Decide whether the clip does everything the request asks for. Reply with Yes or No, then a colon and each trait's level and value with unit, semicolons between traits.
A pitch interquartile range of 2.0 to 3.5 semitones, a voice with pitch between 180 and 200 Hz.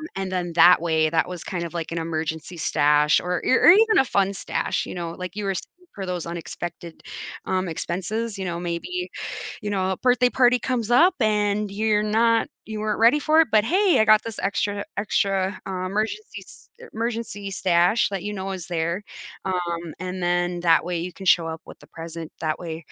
No: average, 4.0 semitones; high, 190 Hz